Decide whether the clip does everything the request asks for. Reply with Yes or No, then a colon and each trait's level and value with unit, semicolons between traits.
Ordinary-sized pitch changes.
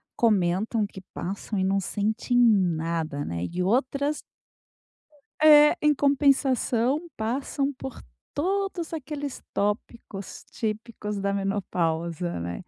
No: wide, 6.7 semitones